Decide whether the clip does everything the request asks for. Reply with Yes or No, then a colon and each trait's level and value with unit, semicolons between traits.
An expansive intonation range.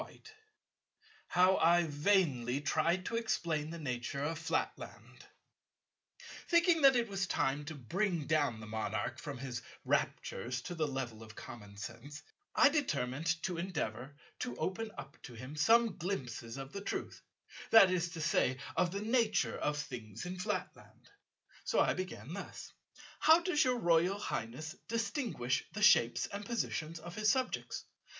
Yes: wide, 7.4 semitones